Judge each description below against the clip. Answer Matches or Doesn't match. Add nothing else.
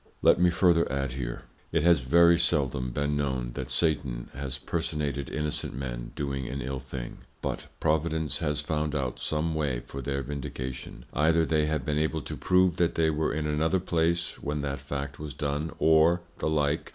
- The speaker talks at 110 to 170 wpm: Doesn't match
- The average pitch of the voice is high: Doesn't match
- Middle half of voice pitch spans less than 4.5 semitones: Matches